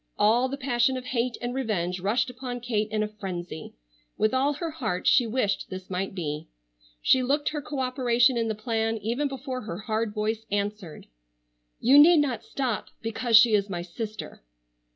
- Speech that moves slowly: No, average, 180 wpm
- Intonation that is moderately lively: Yes, average, 3.6 semitones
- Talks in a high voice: Yes, high, 230 Hz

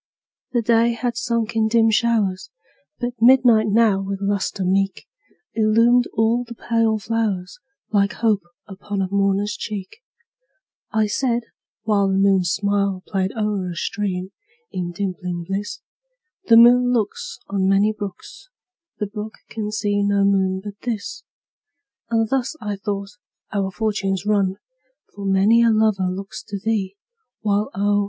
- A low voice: No, high, 205 Hz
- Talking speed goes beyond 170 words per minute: No, average, 145 wpm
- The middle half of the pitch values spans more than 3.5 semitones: No, narrow, 2.5 semitones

